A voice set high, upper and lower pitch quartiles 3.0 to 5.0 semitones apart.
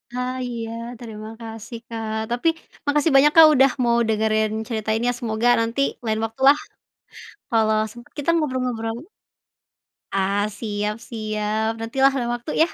No: high, 225 Hz; narrow, 2.5 semitones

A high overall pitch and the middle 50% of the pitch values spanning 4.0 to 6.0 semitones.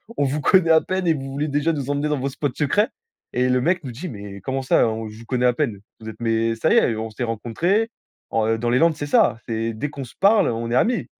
No: low, 130 Hz; average, 5.0 semitones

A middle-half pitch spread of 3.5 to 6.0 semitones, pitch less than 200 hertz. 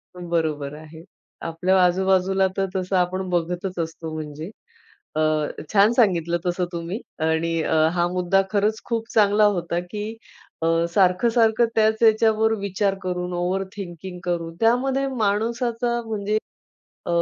Yes: average, 3.9 semitones; high, 190 Hz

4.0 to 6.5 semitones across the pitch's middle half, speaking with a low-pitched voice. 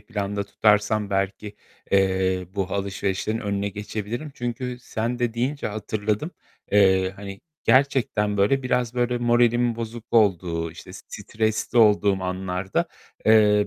No: average, 3.2 semitones; low, 105 Hz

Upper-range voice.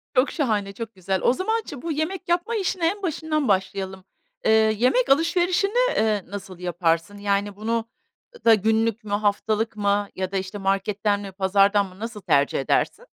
Yes: high, 210 Hz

